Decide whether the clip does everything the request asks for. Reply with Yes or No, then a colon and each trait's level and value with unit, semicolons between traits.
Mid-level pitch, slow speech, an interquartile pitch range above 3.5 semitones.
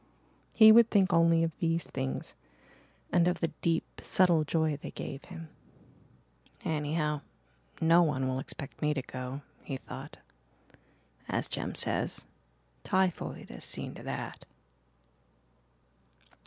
No: medium, 165 Hz; slow, 125 wpm; average, 3.0 semitones